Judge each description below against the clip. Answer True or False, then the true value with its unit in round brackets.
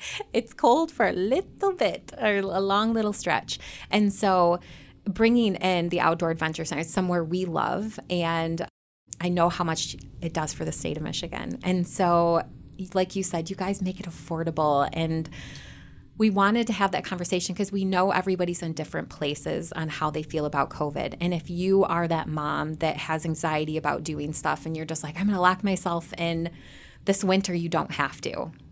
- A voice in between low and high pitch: True (175 Hz)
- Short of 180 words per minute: False (190 wpm)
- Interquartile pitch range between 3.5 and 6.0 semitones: False (2.9 semitones)